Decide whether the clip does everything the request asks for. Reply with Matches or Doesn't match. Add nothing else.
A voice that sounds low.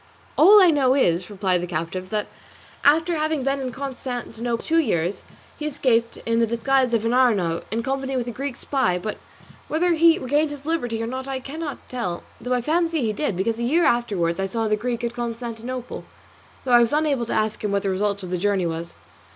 Doesn't match